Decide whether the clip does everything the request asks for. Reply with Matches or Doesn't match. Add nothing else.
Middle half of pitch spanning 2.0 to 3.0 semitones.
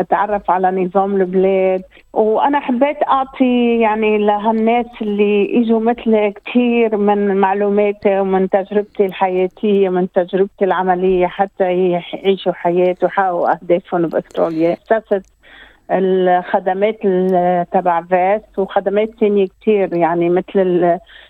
Matches